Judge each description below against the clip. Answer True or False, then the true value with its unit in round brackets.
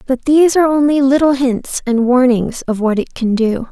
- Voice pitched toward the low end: False (260 Hz)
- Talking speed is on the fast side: True (210 wpm)